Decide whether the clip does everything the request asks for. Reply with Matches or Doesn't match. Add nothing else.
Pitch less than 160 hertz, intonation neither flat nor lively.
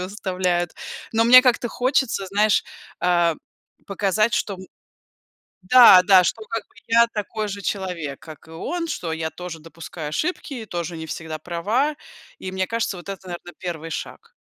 Doesn't match